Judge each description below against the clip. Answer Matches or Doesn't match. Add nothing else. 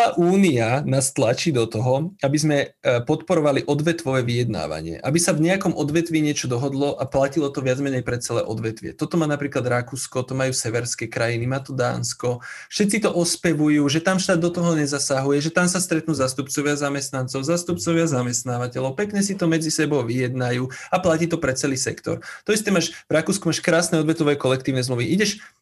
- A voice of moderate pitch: Matches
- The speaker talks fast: Matches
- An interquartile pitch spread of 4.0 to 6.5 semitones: Matches